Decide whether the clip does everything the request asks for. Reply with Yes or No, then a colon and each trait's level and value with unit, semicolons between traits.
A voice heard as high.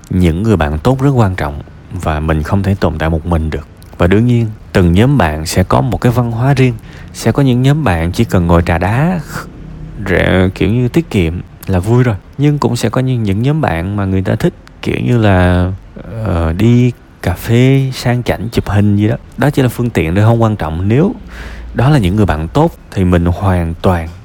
No: low, 100 Hz